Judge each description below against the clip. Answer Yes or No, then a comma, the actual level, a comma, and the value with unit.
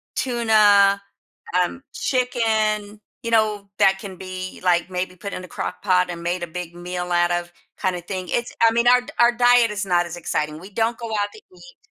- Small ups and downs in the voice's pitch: No, average, 4.1 semitones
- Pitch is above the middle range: Yes, high, 200 Hz